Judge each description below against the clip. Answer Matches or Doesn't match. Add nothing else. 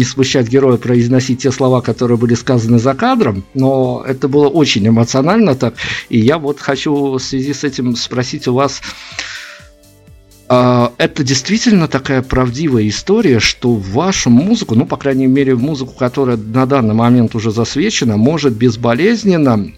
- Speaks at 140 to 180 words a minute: Matches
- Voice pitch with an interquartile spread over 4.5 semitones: Doesn't match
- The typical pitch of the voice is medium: Doesn't match